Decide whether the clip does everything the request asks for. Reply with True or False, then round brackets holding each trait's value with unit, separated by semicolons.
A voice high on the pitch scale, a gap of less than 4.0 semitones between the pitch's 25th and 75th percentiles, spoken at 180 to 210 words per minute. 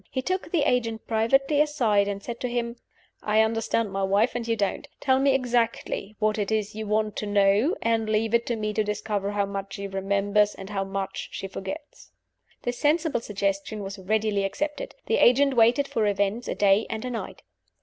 True (220 Hz; 3.3 semitones; 200 wpm)